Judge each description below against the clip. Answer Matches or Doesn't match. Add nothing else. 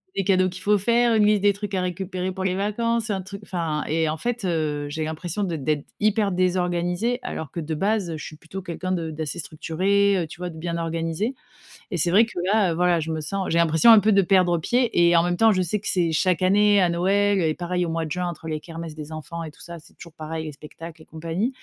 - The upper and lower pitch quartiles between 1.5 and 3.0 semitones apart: Doesn't match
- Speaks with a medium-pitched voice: Matches